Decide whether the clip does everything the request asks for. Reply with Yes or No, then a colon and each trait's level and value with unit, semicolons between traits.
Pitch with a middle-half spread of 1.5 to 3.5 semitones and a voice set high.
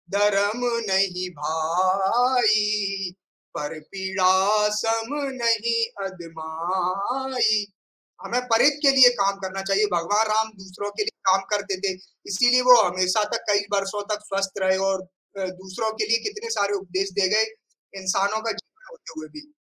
Yes: average, 3.1 semitones; high, 200 Hz